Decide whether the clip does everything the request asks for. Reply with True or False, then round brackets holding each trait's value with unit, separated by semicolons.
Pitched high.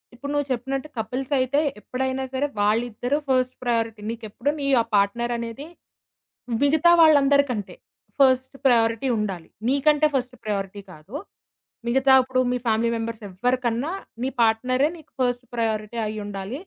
True (245 Hz)